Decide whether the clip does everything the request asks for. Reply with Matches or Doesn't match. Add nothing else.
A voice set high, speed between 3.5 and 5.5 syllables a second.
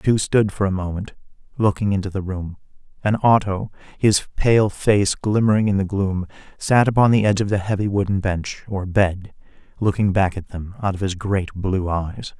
Doesn't match